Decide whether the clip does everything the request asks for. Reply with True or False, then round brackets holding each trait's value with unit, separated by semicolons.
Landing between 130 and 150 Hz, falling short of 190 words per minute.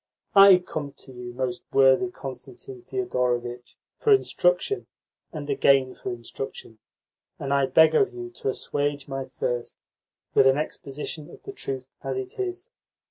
True (135 Hz; 140 wpm)